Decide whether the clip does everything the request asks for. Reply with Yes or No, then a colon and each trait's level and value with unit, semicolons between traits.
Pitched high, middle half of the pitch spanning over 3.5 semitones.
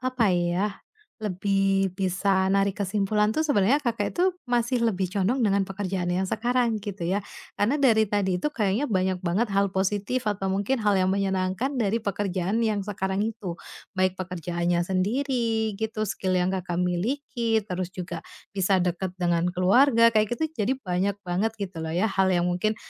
No: high, 195 Hz; average, 3.2 semitones